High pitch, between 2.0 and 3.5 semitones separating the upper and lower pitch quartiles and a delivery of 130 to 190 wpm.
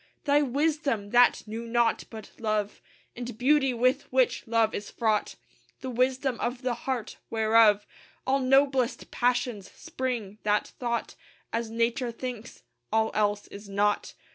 Yes: high, 235 Hz; average, 2.8 semitones; average, 140 wpm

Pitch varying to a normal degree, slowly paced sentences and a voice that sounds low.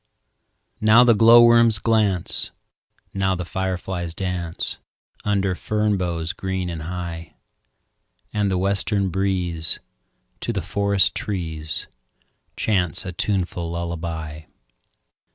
Yes: average, 3.0 semitones; slow, 100 wpm; very low, 95 Hz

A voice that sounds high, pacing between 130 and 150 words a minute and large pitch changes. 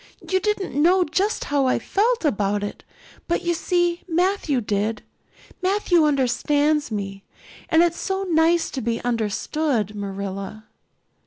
Yes: very high, 295 Hz; slow, 135 wpm; wide, 8.4 semitones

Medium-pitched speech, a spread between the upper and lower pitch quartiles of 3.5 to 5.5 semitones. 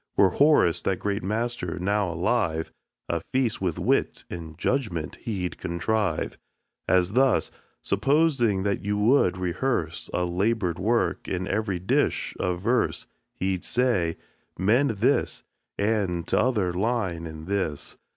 No: very low, 95 Hz; average, 4.7 semitones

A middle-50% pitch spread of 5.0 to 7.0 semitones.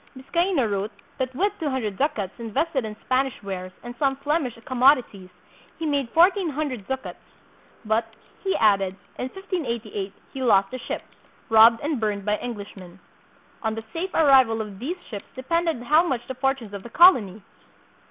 Yes: wide, 5.5 semitones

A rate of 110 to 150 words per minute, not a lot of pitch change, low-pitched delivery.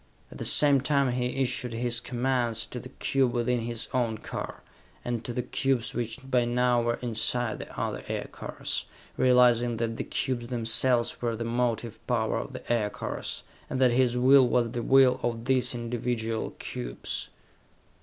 No: average, 165 wpm; narrow, 1.4 semitones; low, 120 Hz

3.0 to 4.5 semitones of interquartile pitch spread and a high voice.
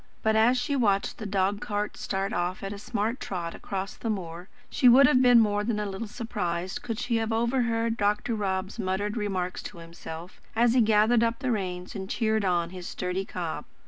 Yes: average, 3.5 semitones; high, 205 Hz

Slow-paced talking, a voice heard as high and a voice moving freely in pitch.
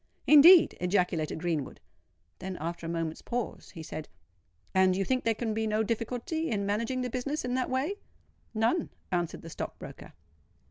No: average, 170 wpm; high, 220 Hz; wide, 6.3 semitones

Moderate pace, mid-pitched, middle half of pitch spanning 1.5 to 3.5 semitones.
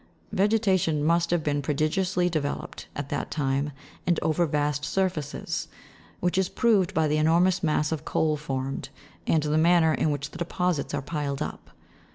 Yes: average, 170 wpm; medium, 155 Hz; average, 3.2 semitones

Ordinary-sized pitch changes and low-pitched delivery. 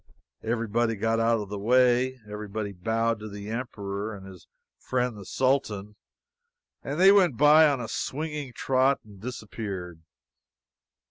Yes: average, 3.9 semitones; low, 115 Hz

